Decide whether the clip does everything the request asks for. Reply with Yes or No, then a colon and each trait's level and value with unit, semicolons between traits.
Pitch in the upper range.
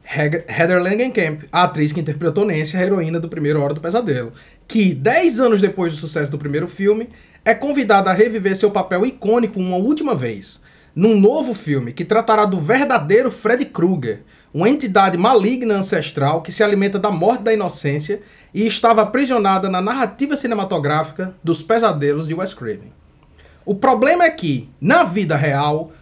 Yes: high, 195 Hz